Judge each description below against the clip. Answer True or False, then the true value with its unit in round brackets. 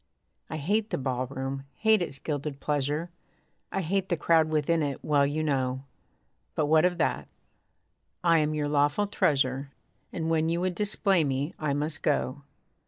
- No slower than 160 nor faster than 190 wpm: True (165 wpm)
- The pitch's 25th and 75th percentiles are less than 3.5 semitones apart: True (3.1 semitones)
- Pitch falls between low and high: True (150 Hz)